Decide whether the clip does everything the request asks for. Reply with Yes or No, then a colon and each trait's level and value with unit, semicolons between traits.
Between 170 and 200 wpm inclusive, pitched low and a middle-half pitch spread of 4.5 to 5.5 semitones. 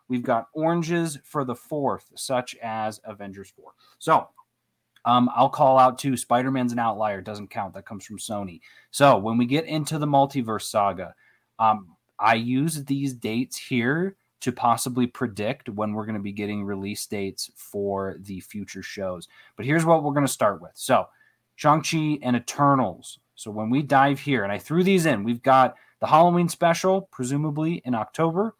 Yes: average, 180 wpm; low, 125 Hz; average, 5.2 semitones